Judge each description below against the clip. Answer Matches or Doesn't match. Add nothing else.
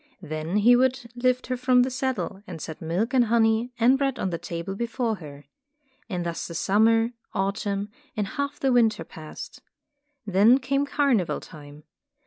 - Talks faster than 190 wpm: Doesn't match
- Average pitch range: Doesn't match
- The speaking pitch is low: Doesn't match